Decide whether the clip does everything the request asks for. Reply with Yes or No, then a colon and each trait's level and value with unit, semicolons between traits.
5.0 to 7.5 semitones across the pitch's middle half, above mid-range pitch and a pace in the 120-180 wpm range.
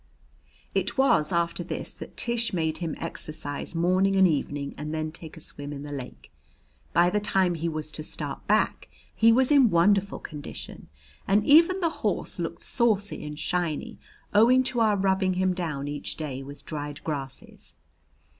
No: wide, 5.4 semitones; medium, 170 Hz; average, 170 wpm